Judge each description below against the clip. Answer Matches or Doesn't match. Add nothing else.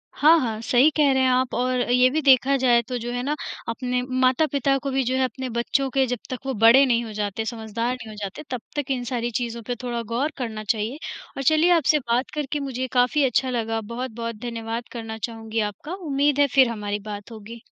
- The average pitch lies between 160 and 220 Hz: Doesn't match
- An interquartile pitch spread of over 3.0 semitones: Doesn't match